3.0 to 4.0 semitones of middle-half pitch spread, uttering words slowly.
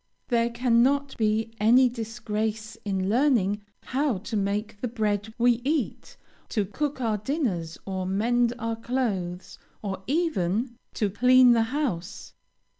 Yes: average, 3.4 semitones; slow, 130 wpm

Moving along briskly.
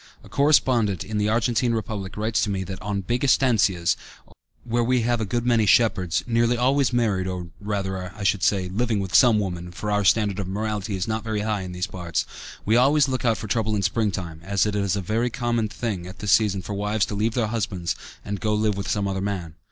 Yes: fast, 230 wpm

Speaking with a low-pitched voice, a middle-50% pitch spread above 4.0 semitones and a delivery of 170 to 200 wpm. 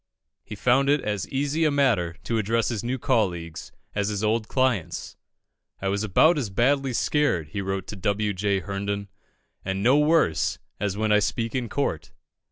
Yes: low, 105 Hz; average, 4.9 semitones; average, 175 wpm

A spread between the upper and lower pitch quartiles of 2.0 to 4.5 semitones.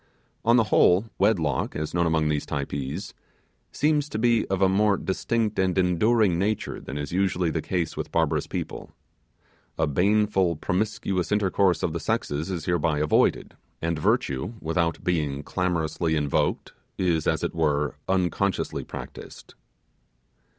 Yes: average, 4.1 semitones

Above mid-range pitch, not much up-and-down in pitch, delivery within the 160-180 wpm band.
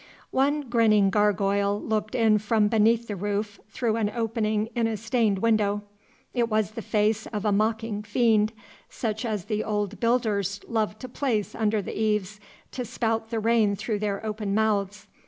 Yes: high, 215 Hz; narrow, 1.6 semitones; average, 170 wpm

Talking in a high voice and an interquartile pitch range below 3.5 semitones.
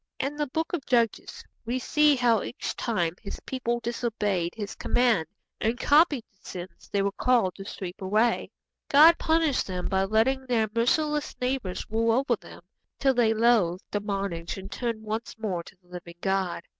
No: high, 225 Hz; average, 4.6 semitones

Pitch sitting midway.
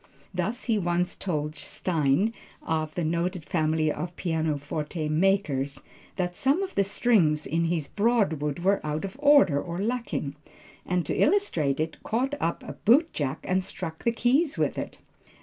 Yes: medium, 175 Hz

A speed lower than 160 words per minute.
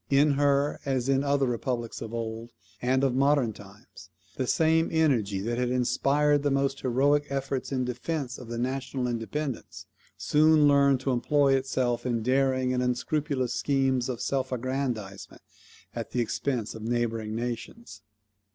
Yes: average, 150 wpm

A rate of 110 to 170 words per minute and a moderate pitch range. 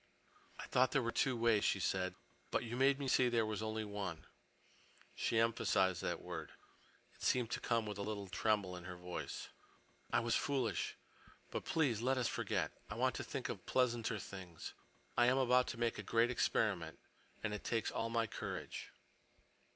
No: average, 185 wpm; average, 3.5 semitones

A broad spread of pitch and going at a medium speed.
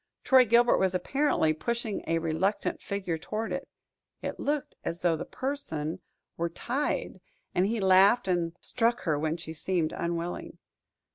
Yes: wide, 6.0 semitones; average, 150 wpm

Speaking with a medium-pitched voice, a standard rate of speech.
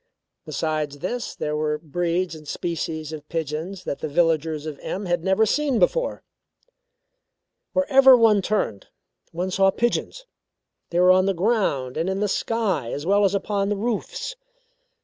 Yes: medium, 180 Hz; average, 155 wpm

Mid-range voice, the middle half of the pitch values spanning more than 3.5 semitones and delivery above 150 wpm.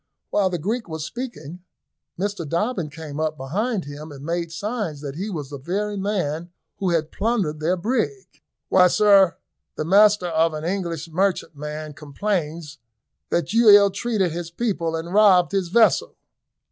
Yes: medium, 175 Hz; average, 4.7 semitones; average, 160 wpm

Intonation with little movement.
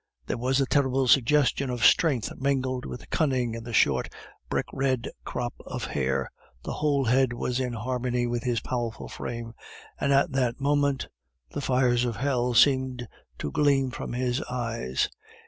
Yes: narrow, 2.2 semitones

